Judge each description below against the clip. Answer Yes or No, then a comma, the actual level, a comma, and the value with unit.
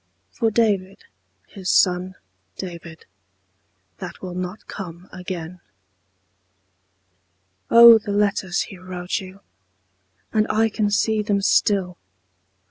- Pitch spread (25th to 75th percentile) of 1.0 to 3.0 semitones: Yes, narrow, 2.6 semitones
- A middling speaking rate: No, slow, 105 wpm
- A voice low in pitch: No, high, 190 Hz